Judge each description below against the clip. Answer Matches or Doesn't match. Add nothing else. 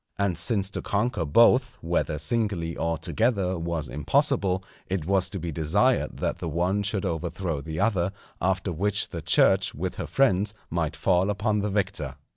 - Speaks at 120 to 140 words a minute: Doesn't match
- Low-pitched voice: Matches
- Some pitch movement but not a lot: Matches